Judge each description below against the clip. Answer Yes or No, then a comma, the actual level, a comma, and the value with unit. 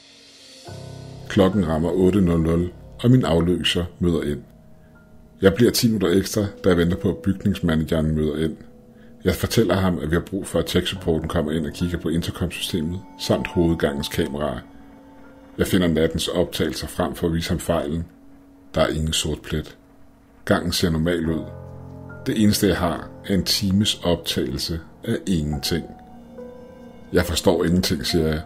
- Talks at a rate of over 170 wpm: No, average, 155 wpm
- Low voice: Yes, very low, 90 Hz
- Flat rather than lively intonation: No, average, 3.8 semitones